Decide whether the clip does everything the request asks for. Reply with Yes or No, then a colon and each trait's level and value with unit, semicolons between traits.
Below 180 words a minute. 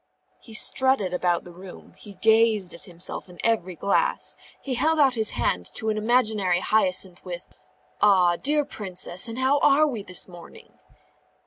Yes: average, 160 wpm